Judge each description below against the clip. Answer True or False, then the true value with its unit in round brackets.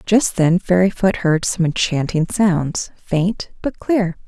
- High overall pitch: False (180 Hz)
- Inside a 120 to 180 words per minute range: True (140 wpm)